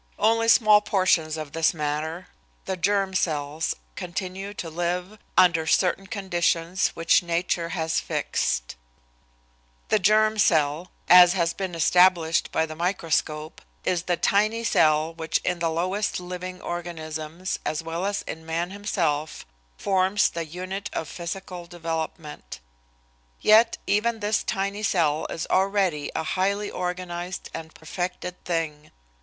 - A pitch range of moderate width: Yes, average, 3.1 semitones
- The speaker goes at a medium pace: No, slow, 130 wpm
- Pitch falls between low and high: Yes, medium, 175 Hz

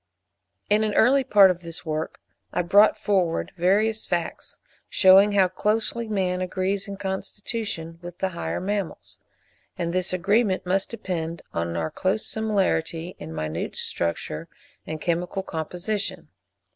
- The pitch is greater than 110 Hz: Yes, medium, 185 Hz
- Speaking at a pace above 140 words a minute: No, slow, 135 wpm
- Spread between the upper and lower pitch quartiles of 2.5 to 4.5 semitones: Yes, average, 3.4 semitones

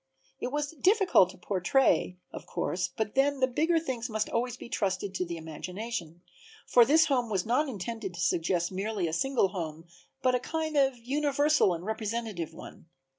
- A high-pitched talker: Yes, high, 230 Hz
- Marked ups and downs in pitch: Yes, wide, 6.7 semitones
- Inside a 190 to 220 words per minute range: No, average, 175 wpm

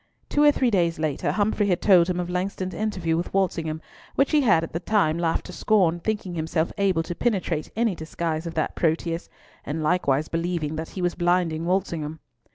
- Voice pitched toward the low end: No, medium, 175 Hz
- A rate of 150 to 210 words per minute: Yes, average, 195 wpm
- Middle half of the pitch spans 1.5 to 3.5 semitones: Yes, average, 3.1 semitones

